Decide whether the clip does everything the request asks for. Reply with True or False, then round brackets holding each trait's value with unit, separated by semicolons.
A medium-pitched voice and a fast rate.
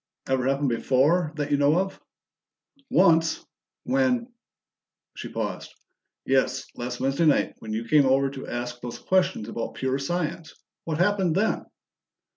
False (145 Hz; 145 wpm)